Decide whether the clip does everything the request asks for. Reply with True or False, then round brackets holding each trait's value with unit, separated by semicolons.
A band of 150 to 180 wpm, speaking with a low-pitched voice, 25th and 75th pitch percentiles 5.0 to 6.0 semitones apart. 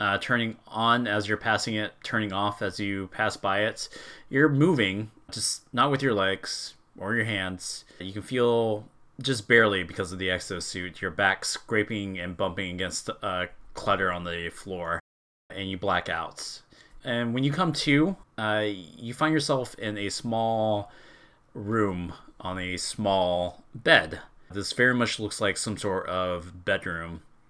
False (160 wpm; 105 Hz; 3.9 semitones)